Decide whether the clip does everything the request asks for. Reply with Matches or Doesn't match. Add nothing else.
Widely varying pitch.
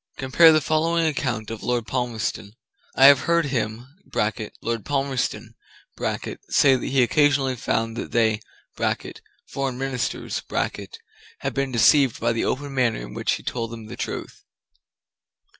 Doesn't match